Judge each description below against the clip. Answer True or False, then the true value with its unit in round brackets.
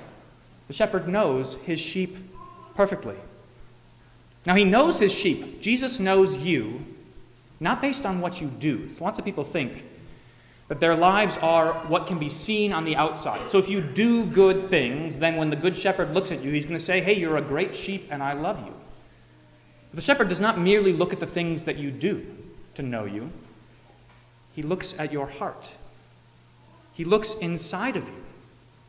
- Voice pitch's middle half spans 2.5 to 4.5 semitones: False (5.2 semitones)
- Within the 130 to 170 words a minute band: False (185 wpm)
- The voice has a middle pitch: True (170 Hz)